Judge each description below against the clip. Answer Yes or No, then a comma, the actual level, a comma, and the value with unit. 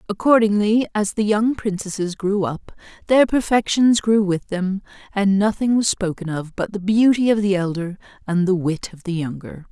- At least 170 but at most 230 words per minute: Yes, average, 180 wpm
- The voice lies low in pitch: No, high, 200 Hz